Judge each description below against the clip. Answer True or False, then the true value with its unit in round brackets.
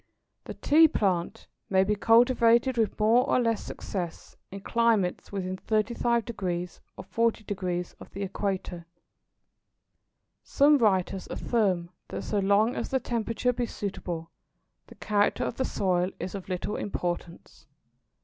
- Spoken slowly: True (130 wpm)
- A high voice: True (205 Hz)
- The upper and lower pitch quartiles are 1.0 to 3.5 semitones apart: False (4.0 semitones)